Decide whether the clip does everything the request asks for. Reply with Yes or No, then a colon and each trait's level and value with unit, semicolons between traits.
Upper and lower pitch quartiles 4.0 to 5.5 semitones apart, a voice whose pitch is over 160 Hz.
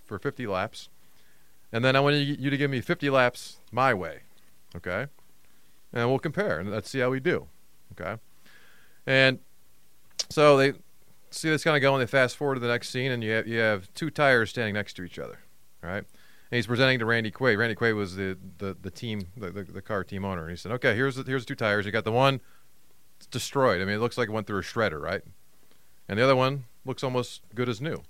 No: average, 4.8 semitones; low, 120 Hz